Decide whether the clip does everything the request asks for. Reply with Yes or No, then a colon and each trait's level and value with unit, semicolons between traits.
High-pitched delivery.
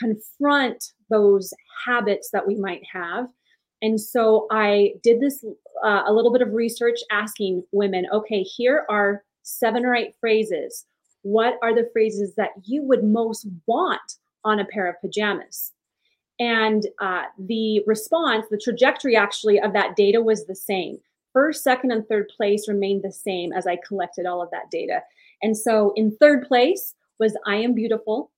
Yes: high, 215 Hz